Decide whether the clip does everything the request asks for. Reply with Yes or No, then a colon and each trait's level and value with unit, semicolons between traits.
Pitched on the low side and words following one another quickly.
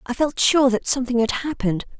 No: very high, 250 Hz; fast, 210 wpm